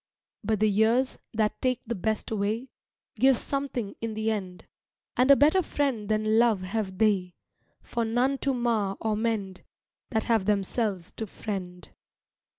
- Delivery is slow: No, average, 155 wpm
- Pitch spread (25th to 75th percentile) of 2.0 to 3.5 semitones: Yes, average, 3.0 semitones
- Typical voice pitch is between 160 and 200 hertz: No, high, 220 Hz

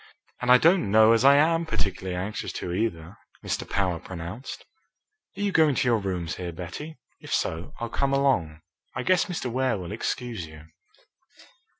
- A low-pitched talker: Yes, low, 110 Hz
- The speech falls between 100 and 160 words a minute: No, average, 175 wpm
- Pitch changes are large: Yes, wide, 7.5 semitones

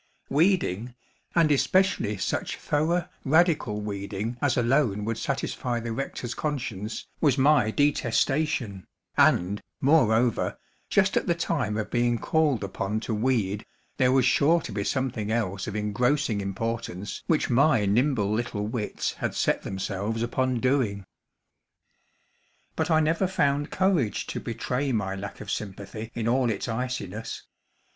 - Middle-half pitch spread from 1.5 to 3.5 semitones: No, wide, 5.4 semitones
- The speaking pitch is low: Yes, low, 120 Hz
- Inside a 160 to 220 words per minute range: No, slow, 135 wpm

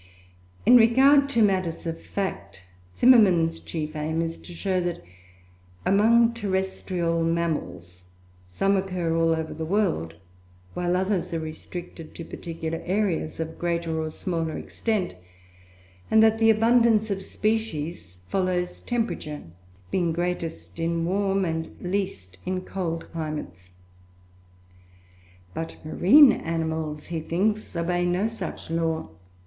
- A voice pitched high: No, medium, 175 Hz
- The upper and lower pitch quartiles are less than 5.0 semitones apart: Yes, average, 3.5 semitones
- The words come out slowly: Yes, slow, 120 wpm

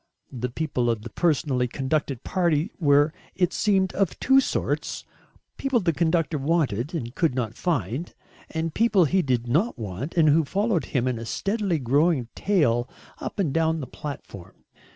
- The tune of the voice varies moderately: No, wide, 5.7 semitones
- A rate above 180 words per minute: No, average, 165 wpm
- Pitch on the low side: No, medium, 155 Hz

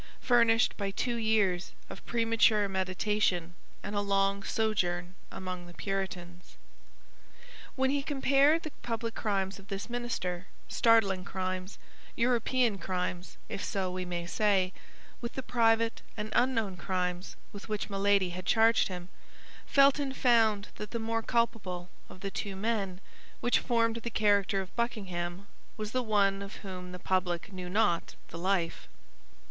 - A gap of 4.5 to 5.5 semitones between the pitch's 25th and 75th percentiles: No, average, 3.7 semitones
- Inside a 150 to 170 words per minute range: No, average, 140 wpm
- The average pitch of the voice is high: Yes, high, 200 Hz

